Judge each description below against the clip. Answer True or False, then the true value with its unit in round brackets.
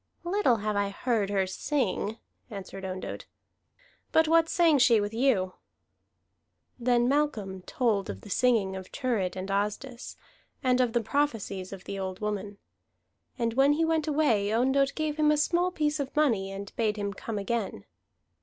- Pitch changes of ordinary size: False (6.2 semitones)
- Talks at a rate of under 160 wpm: False (165 wpm)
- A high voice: True (230 Hz)